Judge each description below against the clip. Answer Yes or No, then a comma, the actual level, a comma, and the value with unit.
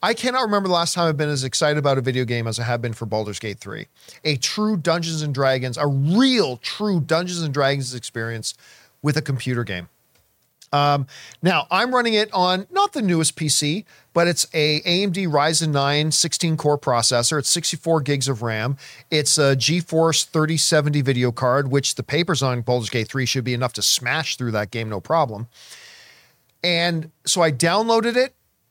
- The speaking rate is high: No, average, 180 wpm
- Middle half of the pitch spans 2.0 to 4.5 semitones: No, average, 4.9 semitones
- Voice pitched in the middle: Yes, medium, 150 Hz